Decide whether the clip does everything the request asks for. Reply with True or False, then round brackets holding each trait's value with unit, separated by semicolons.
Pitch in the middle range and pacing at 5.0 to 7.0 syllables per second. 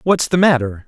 True (150 Hz; 5.2 syllables/s)